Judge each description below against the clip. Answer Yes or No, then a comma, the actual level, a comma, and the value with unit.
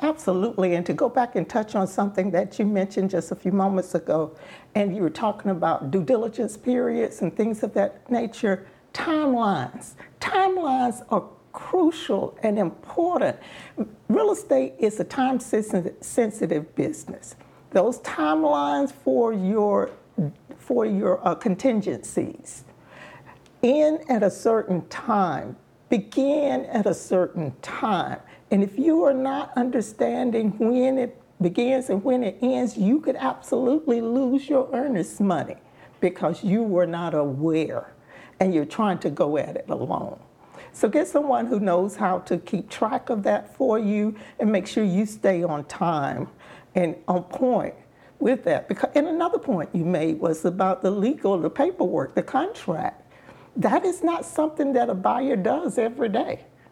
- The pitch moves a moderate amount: No, wide, 5.7 semitones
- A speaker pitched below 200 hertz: No, high, 220 Hz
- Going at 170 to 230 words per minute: No, average, 150 wpm